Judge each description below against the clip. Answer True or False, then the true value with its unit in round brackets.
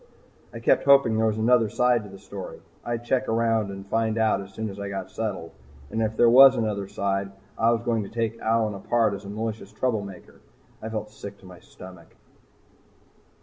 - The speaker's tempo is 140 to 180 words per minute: False (205 wpm)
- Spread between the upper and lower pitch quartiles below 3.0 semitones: True (2.6 semitones)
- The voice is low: True (110 Hz)